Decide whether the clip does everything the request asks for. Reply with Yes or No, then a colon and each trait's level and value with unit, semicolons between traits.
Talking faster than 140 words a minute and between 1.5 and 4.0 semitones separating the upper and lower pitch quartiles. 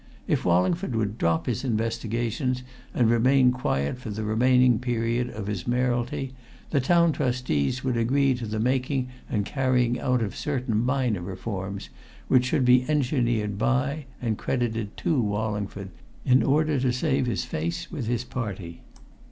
Yes: average, 150 wpm; average, 3.0 semitones